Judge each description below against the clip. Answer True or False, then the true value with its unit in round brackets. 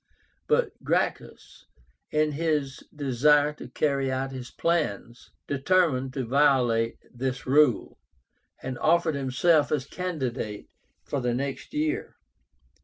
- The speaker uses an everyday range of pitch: True (3.0 semitones)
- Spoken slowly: True (110 wpm)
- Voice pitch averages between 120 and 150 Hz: True (140 Hz)